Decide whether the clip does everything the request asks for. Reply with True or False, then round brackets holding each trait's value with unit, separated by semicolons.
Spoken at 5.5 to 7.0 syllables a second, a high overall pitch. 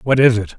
False (6.1 syllables/s; 115 Hz)